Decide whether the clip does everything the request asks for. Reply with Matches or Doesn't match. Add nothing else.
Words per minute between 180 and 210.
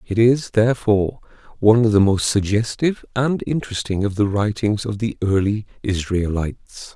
Doesn't match